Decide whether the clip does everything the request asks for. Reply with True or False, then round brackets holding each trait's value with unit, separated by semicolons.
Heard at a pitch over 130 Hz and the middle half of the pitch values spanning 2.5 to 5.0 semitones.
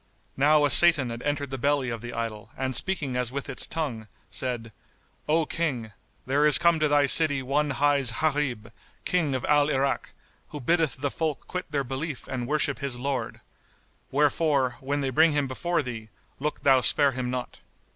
True (140 Hz; 2.8 semitones)